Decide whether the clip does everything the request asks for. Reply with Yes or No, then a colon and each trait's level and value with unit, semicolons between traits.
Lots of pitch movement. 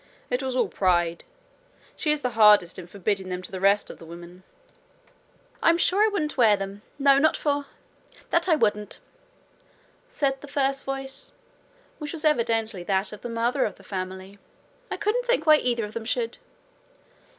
Yes: wide, 6.7 semitones